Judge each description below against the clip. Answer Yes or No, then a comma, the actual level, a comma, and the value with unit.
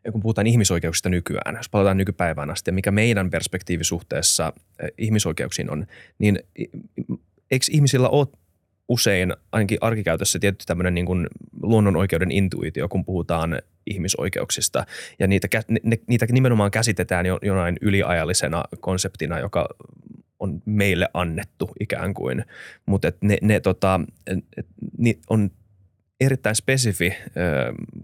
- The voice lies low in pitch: Yes, very low, 95 Hz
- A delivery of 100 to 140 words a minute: Yes, average, 120 wpm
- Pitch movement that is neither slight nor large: Yes, average, 3.6 semitones